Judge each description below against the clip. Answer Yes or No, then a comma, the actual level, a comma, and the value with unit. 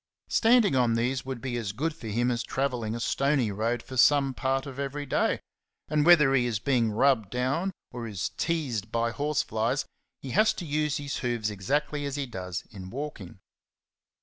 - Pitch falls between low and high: No, low, 130 Hz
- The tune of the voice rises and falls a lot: No, average, 3.8 semitones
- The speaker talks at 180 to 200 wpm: Yes, average, 185 wpm